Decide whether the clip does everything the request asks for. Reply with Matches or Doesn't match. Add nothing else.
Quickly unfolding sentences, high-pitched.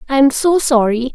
Doesn't match